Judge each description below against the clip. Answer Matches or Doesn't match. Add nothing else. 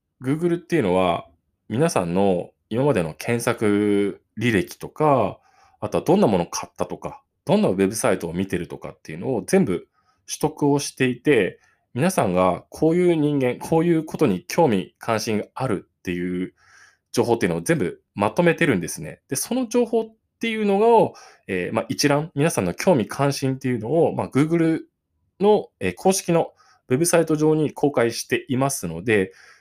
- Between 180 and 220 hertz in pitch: Doesn't match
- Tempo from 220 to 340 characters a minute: Doesn't match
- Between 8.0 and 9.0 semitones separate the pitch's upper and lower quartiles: Matches